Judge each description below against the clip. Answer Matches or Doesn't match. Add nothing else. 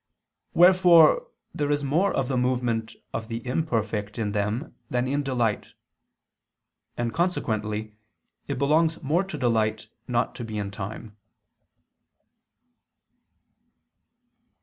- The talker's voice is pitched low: Matches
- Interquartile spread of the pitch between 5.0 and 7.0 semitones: Matches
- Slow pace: Matches